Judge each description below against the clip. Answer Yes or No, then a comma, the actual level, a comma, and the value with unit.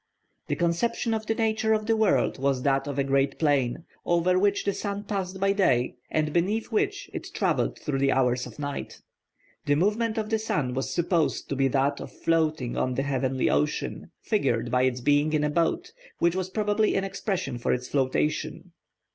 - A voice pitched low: No, medium, 155 Hz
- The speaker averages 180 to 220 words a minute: Yes, average, 195 wpm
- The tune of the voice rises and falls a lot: Yes, wide, 6.7 semitones